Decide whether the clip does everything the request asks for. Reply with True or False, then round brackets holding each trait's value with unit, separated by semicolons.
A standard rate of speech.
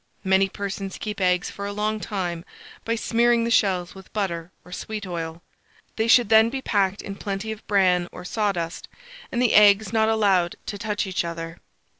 True (185 wpm)